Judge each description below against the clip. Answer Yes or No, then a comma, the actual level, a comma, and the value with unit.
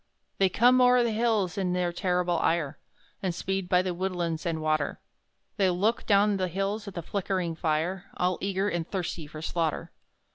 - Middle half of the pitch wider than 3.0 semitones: No, narrow, 2.6 semitones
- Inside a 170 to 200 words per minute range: Yes, average, 180 wpm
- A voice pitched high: No, medium, 180 Hz